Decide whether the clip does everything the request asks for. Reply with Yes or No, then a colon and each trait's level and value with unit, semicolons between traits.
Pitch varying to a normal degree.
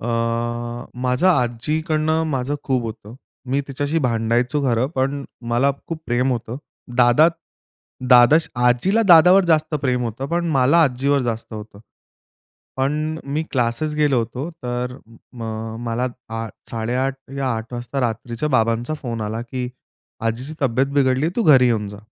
Yes: average, 3.8 semitones